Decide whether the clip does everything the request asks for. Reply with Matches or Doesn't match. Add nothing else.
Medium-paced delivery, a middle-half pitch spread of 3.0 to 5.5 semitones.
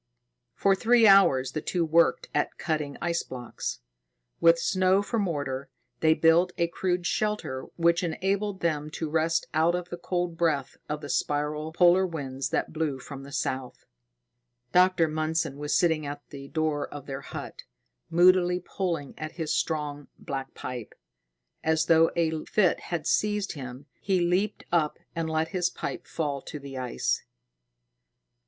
Matches